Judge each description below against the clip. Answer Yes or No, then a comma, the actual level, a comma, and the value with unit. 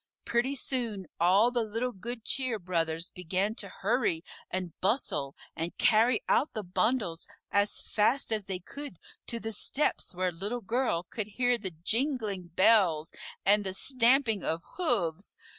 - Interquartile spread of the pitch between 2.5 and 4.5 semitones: No, average, 4.9 semitones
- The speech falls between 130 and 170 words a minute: Yes, average, 150 wpm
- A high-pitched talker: Yes, high, 210 Hz